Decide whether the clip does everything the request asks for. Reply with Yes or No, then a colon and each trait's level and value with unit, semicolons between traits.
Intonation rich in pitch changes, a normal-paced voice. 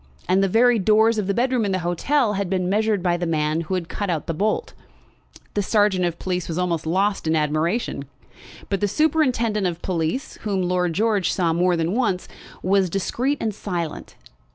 No: average, 3.8 semitones; average, 195 wpm